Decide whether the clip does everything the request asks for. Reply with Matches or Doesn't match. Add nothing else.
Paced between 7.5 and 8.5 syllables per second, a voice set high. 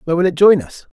Doesn't match